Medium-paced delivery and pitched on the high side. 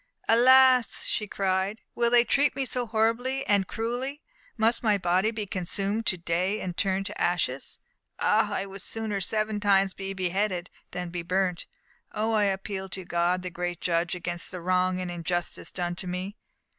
Yes: average, 175 wpm; high, 195 Hz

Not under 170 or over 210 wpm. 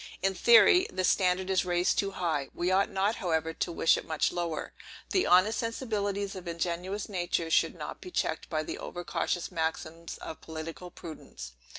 Yes: average, 180 wpm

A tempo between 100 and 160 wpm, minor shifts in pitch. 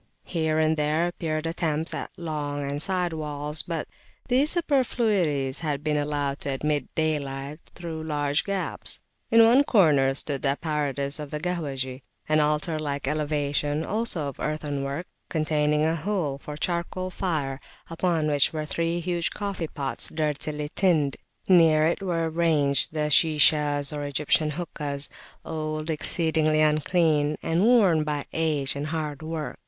Yes: average, 150 wpm; narrow, 2.3 semitones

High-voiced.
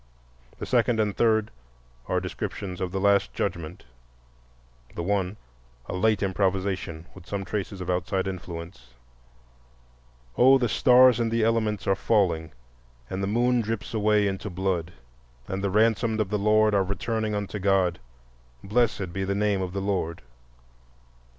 No: low, 100 Hz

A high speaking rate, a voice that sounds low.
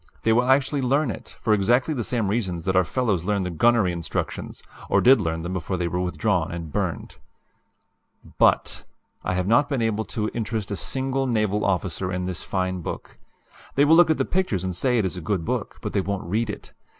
Yes: fast, 220 wpm; low, 105 Hz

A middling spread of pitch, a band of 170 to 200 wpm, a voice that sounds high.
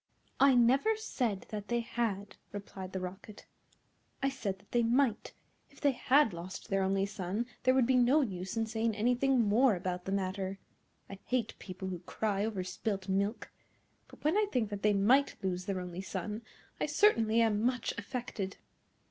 Yes: average, 4.2 semitones; average, 180 wpm; high, 210 Hz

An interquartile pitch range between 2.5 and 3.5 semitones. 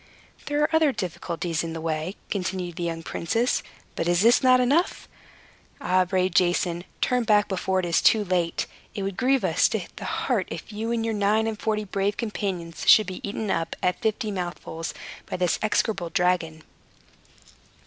No: average, 4.0 semitones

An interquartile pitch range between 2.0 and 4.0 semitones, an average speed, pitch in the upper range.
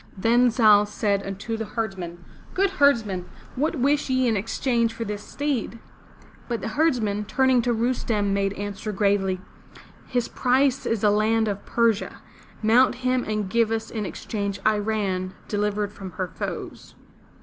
Yes: average, 3.1 semitones; average, 155 wpm; high, 220 Hz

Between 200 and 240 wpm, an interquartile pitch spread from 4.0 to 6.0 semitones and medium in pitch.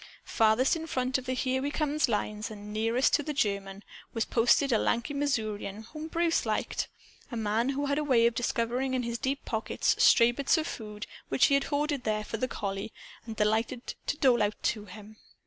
No: fast, 205 wpm; average, 4.3 semitones; high, 235 Hz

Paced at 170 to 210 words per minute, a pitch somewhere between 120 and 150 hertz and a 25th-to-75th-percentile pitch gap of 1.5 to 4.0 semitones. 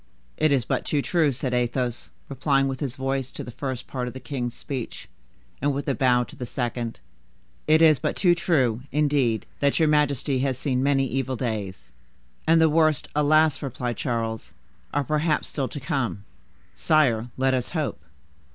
Yes: average, 180 wpm; low, 135 Hz; average, 3.2 semitones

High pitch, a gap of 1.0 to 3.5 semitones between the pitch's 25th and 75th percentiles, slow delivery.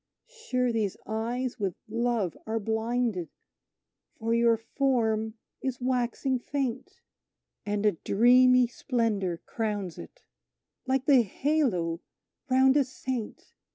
Yes: high, 235 Hz; average, 3.0 semitones; slow, 110 wpm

